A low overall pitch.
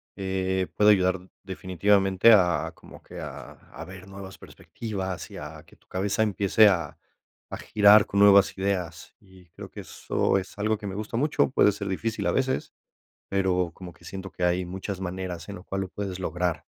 Yes: very low, 95 Hz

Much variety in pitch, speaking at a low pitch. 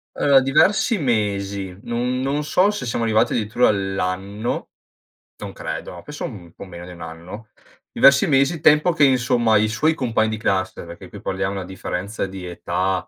Yes: wide, 6.1 semitones; low, 110 Hz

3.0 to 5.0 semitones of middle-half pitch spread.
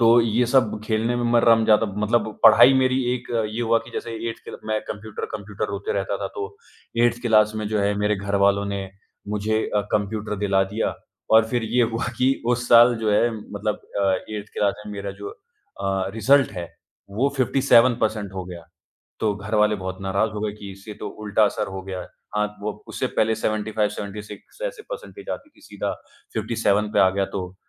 No: narrow, 2.4 semitones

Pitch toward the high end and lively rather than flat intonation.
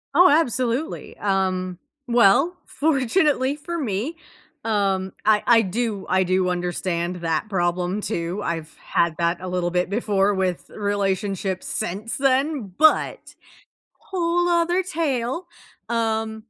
Yes: high, 205 Hz; wide, 6.5 semitones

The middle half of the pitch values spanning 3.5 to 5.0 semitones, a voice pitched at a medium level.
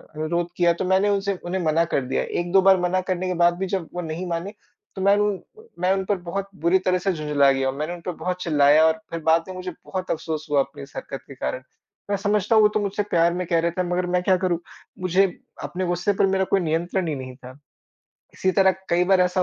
No: average, 2.7 semitones; medium, 180 Hz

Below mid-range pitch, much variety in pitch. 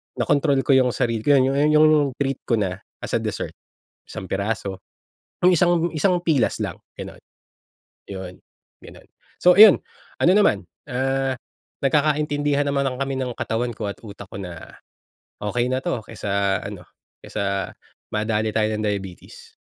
Yes: low, 125 Hz; wide, 6.2 semitones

